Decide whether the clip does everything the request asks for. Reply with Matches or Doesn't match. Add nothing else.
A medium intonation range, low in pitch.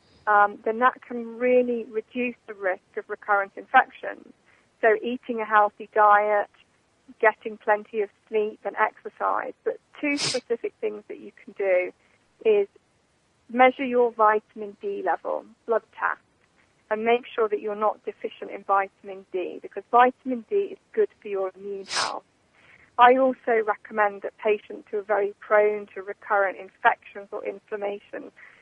Doesn't match